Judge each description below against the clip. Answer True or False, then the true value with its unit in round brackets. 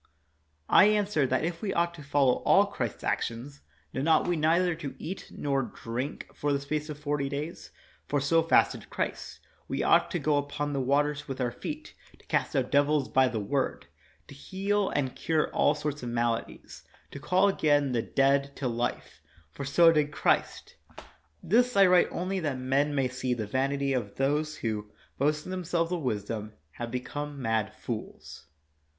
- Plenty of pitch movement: False (3.8 semitones)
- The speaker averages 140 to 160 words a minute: False (180 wpm)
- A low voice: False (145 Hz)